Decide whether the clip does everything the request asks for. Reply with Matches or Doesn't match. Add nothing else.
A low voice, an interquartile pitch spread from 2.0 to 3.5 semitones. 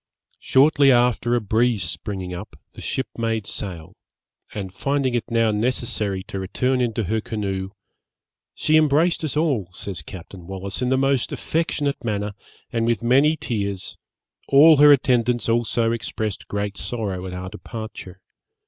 Doesn't match